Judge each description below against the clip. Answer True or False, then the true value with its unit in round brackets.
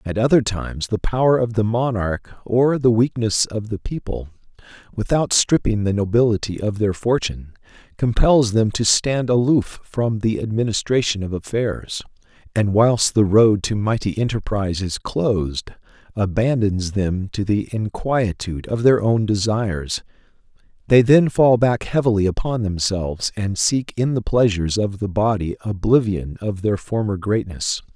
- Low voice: True (110 Hz)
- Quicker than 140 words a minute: True (150 wpm)